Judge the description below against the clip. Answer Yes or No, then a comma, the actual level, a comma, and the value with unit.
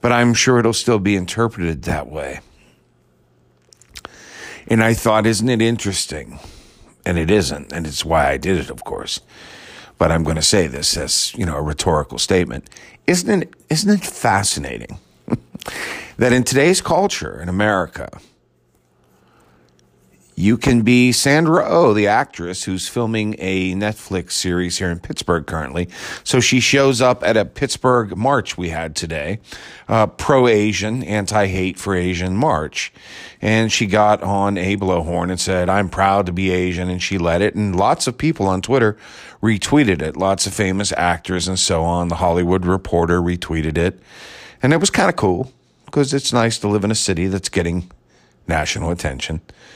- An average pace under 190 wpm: Yes, average, 170 wpm